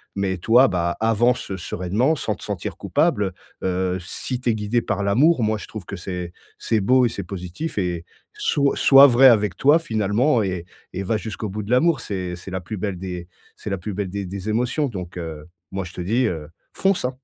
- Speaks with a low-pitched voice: Yes, low, 100 Hz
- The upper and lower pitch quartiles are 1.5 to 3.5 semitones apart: No, average, 4.7 semitones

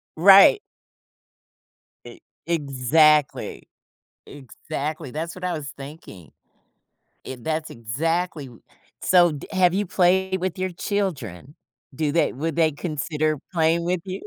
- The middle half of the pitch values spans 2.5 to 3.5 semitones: No, average, 3.9 semitones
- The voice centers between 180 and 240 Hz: No, medium, 160 Hz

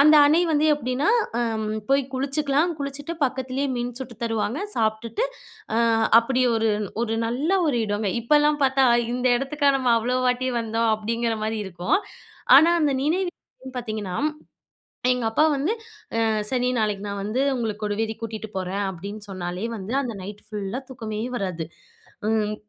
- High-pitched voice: Yes, high, 235 Hz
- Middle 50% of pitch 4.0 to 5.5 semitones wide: Yes, average, 4.3 semitones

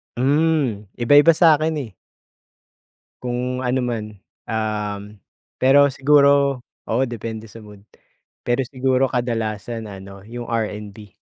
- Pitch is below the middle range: Yes, low, 120 Hz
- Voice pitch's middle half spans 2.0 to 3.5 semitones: No, average, 3.9 semitones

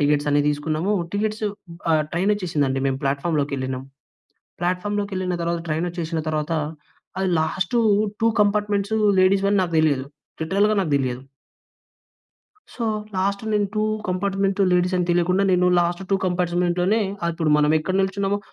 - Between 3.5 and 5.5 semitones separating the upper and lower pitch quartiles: Yes, average, 4.2 semitones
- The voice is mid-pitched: Yes, medium, 180 Hz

